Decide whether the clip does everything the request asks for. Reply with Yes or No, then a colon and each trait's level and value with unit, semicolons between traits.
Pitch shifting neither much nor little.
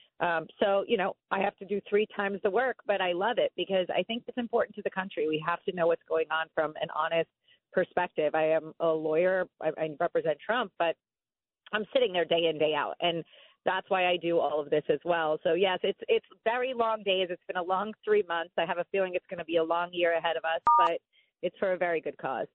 Yes: average, 3.6 semitones